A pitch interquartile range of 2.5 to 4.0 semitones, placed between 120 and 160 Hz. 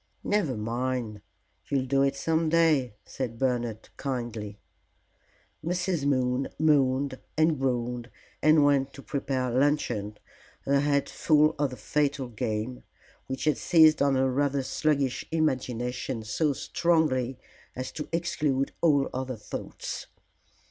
Yes: average, 3.2 semitones; low, 135 Hz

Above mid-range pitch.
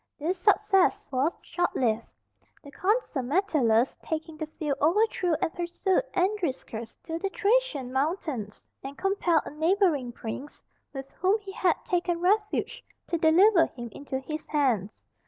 Yes: very high, 320 Hz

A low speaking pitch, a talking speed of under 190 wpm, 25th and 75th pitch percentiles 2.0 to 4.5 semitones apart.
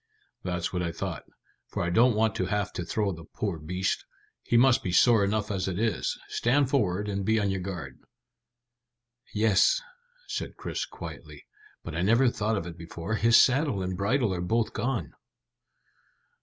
Yes: low, 100 Hz; average, 175 wpm; average, 4.0 semitones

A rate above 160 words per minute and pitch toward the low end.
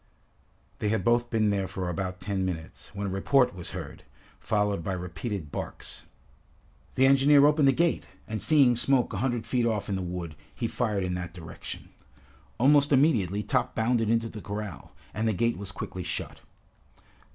Yes: average, 175 wpm; low, 105 Hz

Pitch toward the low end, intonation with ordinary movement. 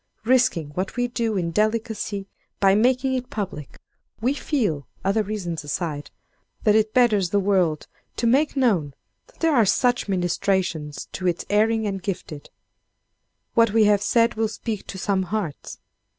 No: high, 205 Hz; average, 4.2 semitones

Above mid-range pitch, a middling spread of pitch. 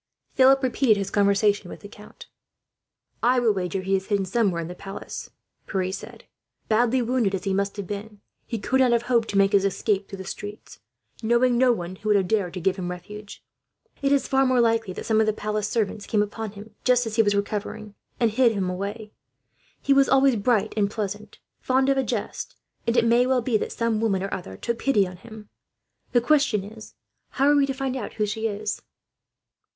Yes: high, 215 Hz; average, 3.3 semitones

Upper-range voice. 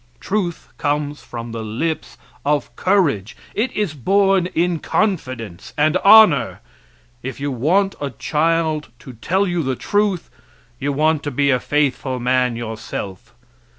No: medium, 150 Hz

